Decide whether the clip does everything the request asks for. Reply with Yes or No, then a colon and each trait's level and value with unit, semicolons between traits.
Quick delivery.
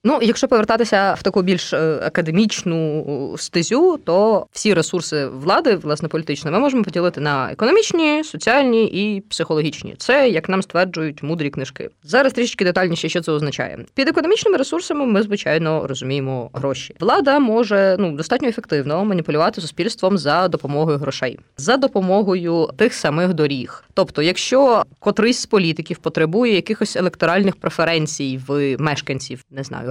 No: average, 140 wpm